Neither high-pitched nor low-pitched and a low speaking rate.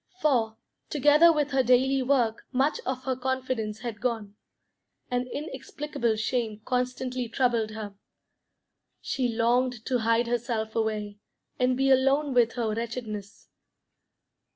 No: high, 245 Hz; slow, 125 wpm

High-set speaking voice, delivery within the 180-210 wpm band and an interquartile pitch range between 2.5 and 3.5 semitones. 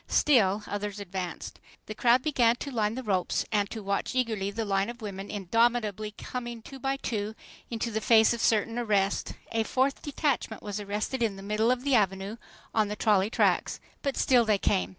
Yes: high, 220 Hz; average, 190 wpm; average, 2.9 semitones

